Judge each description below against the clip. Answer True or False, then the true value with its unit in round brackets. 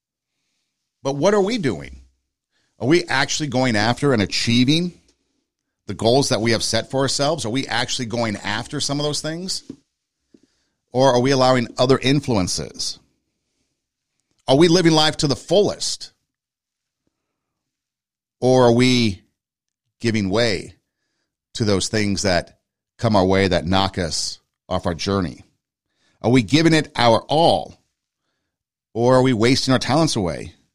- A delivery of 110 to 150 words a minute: True (140 wpm)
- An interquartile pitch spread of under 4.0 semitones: False (5.6 semitones)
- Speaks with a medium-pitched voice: False (120 Hz)